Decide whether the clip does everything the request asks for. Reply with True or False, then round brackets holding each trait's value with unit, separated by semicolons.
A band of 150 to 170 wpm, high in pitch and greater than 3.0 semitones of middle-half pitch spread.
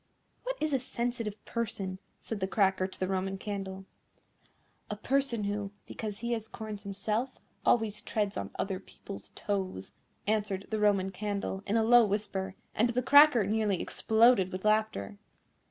False (155 wpm; 210 Hz; 2.7 semitones)